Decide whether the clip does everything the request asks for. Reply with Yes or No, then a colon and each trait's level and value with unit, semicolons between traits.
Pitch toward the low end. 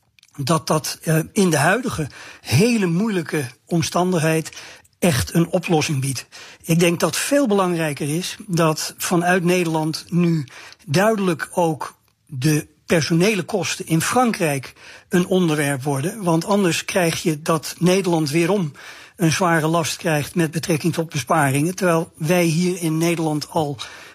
No: medium, 165 Hz